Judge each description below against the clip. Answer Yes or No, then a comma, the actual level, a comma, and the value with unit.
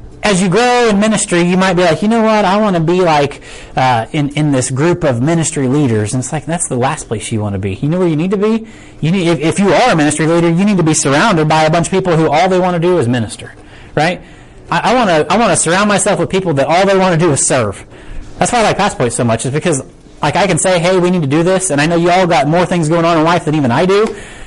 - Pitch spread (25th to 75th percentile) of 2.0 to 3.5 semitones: No, average, 4.4 semitones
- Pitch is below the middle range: No, medium, 170 Hz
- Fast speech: Yes, fast, 305 wpm